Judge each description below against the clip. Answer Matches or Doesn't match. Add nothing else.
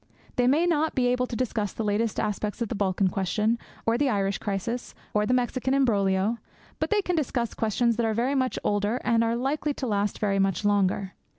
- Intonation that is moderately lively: Matches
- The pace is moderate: Doesn't match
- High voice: Matches